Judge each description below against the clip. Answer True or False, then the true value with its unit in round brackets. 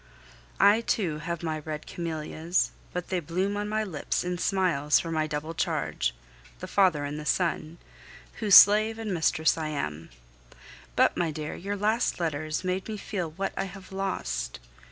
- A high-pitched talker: False (170 Hz)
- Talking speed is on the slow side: False (170 wpm)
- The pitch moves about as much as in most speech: True (4.1 semitones)